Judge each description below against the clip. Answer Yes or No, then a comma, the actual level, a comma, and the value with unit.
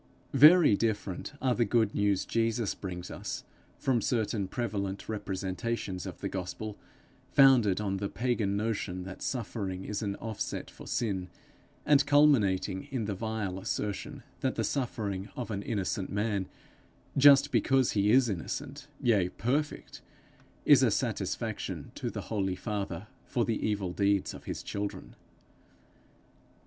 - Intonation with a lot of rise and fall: No, average, 3.8 semitones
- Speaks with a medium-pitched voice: No, low, 105 Hz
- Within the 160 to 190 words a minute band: No, average, 140 wpm